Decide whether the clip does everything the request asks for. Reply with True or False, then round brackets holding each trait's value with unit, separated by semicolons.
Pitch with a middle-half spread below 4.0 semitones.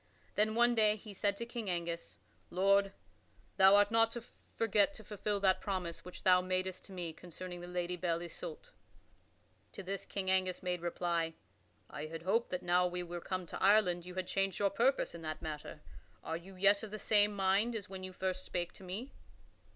True (2.5 semitones)